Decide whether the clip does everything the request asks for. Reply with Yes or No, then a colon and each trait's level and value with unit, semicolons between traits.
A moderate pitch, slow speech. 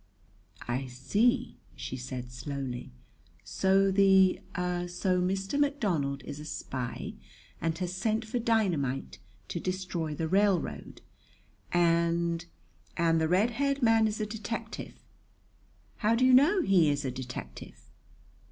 Yes: medium, 180 Hz; slow, 125 wpm